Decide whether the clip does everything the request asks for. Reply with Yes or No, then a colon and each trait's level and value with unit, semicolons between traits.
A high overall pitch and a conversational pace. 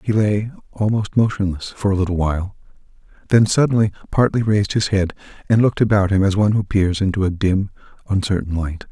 No: low, 100 Hz; average, 180 wpm